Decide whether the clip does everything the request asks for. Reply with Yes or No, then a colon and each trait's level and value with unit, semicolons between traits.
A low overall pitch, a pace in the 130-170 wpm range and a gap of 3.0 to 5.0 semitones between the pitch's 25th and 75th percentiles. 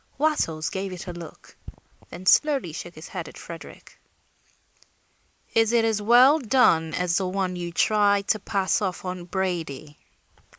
No: high, 190 Hz; average, 155 wpm; average, 4.0 semitones